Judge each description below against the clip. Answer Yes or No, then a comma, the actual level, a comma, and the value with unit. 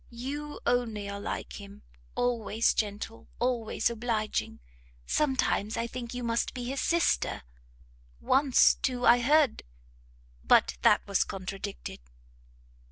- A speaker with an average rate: No, slow, 115 wpm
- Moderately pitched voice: No, high, 235 Hz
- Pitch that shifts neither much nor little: Yes, average, 3.2 semitones